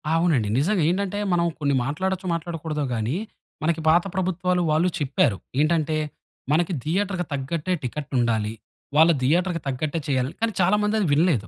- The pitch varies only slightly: No, average, 4.2 semitones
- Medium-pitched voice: Yes, medium, 165 Hz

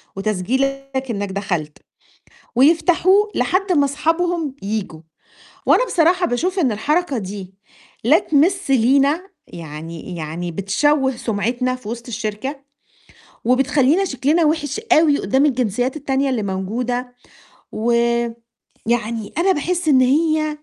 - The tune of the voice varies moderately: No, wide, 6.5 semitones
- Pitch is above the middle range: Yes, very high, 265 Hz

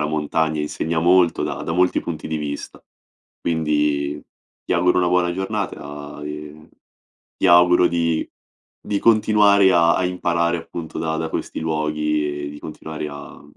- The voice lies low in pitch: Yes, very low, 80 Hz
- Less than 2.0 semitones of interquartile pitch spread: No, average, 2.7 semitones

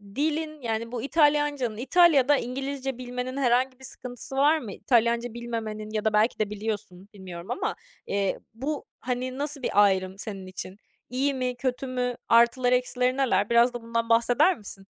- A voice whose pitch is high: Yes, high, 245 Hz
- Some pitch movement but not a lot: Yes, average, 3.5 semitones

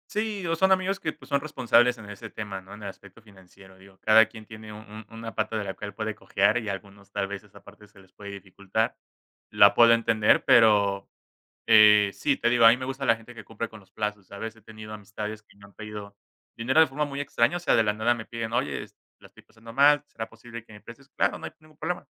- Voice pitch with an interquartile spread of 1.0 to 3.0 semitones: Yes, narrow, 2.6 semitones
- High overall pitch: No, low, 110 Hz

